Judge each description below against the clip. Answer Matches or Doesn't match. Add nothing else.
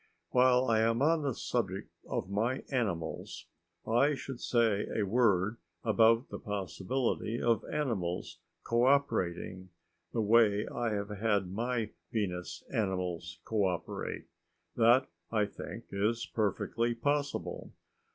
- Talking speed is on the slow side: Matches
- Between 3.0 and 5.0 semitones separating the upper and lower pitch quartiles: Matches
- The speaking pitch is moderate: Doesn't match